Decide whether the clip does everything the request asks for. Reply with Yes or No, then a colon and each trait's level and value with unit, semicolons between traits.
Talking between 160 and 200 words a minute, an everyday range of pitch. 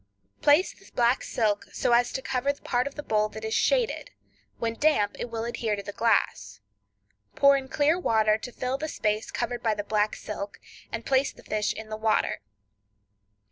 Yes: average, 195 wpm; average, 3.9 semitones